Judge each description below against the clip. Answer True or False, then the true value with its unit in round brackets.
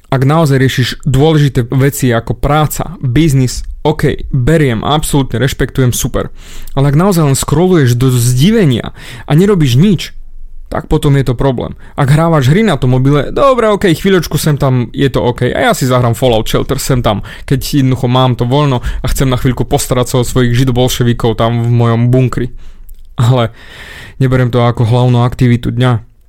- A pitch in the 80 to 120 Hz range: False (130 Hz)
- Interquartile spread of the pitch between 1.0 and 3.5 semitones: True (2.9 semitones)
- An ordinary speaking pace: False (170 wpm)